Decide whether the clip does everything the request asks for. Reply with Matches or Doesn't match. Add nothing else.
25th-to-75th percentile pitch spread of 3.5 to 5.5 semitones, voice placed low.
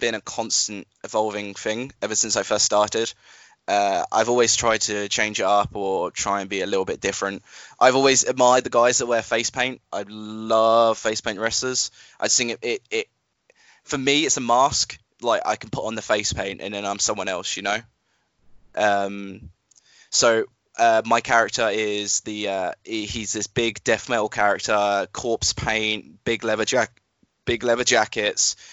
Doesn't match